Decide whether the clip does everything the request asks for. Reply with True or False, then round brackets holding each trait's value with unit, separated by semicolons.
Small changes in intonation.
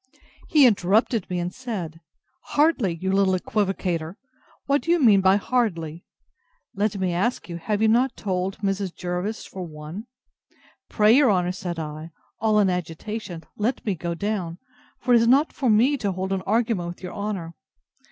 False (3.9 semitones)